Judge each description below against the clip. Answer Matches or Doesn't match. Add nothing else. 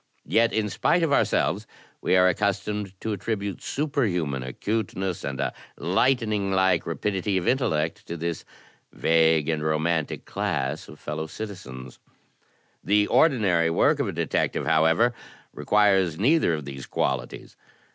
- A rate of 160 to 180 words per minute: Doesn't match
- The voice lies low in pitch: Matches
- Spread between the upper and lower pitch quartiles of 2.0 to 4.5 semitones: Doesn't match